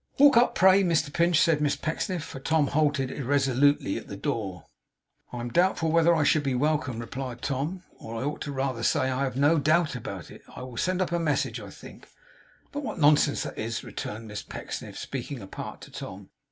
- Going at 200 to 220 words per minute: Yes, fast, 205 wpm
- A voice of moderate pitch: Yes, medium, 145 Hz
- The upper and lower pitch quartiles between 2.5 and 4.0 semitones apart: No, average, 4.4 semitones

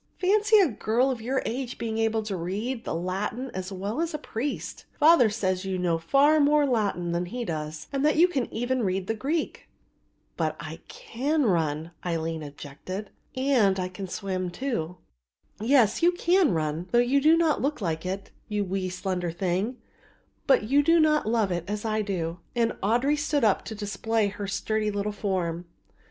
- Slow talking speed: No, average, 185 wpm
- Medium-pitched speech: No, high, 215 Hz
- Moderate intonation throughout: No, wide, 6.5 semitones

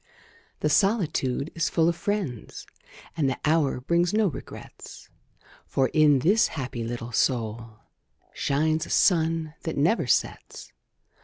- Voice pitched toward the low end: No, medium, 155 Hz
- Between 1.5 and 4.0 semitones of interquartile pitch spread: No, average, 4.7 semitones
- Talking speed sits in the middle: No, slow, 130 wpm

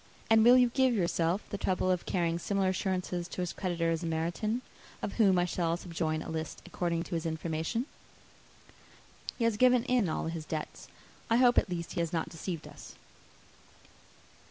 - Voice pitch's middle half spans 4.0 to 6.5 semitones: Yes, average, 4.4 semitones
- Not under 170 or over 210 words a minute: Yes, average, 180 wpm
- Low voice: No, medium, 175 Hz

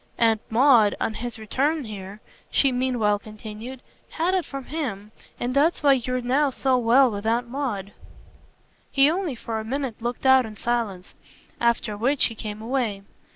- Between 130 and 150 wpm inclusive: No, average, 165 wpm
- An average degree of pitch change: Yes, average, 3.8 semitones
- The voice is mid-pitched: No, high, 240 Hz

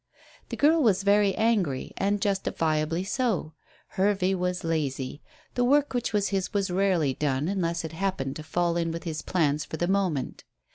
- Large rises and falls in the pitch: No, average, 4.0 semitones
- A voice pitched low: No, medium, 180 Hz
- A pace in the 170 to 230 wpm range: Yes, average, 175 wpm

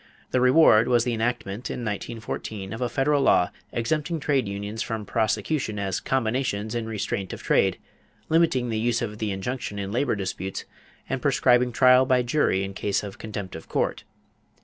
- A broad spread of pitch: No, average, 3.8 semitones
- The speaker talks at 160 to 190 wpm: Yes, average, 170 wpm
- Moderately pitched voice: No, low, 115 Hz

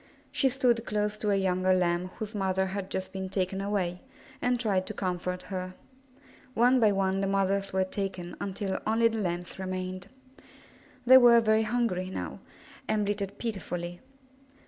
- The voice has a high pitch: Yes, high, 195 Hz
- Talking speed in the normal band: Yes, average, 160 wpm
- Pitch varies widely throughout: No, narrow, 2.6 semitones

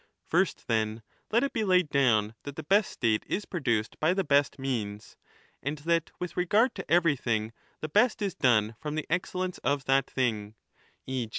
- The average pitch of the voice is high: No, medium, 145 Hz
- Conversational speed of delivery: Yes, average, 180 wpm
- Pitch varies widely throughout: Yes, wide, 7.5 semitones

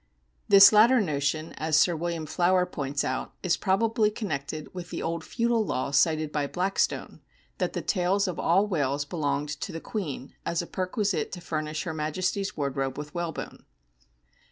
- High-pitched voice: No, medium, 165 Hz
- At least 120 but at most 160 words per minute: No, average, 170 wpm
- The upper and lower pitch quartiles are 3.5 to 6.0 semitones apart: Yes, average, 4.2 semitones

